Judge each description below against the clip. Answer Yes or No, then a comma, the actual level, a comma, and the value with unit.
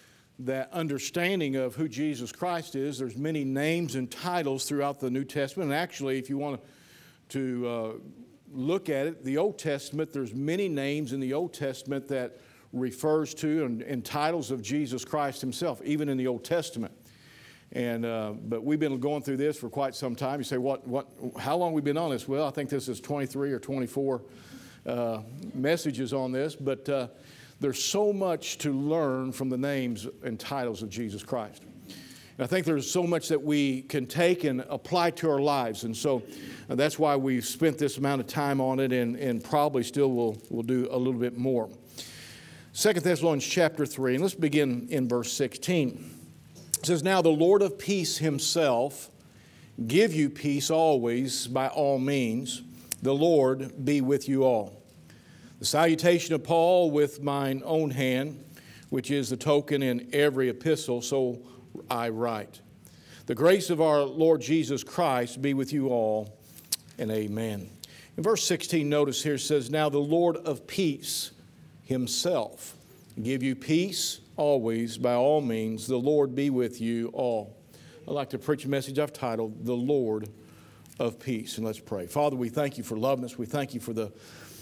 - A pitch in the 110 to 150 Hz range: Yes, medium, 140 Hz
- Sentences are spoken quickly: No, average, 180 wpm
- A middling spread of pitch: Yes, average, 3.3 semitones